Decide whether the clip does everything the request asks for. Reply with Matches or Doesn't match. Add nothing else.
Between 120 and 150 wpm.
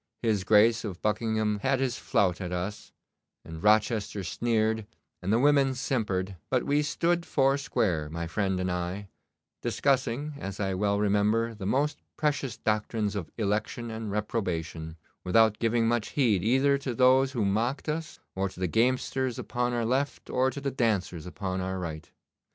Doesn't match